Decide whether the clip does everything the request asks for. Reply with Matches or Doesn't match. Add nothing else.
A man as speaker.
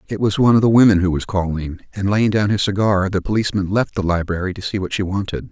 Matches